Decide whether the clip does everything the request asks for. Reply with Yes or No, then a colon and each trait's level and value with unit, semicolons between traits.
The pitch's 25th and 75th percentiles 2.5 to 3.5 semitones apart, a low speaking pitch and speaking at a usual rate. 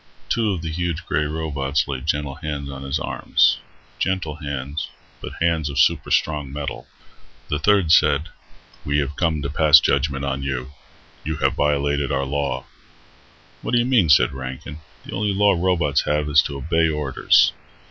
Yes: average, 2.8 semitones; very low, 75 Hz; average, 170 wpm